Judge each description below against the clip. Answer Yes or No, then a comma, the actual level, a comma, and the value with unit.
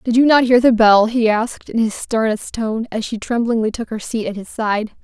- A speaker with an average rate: No, fast, 250 wpm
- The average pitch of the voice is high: Yes, high, 225 Hz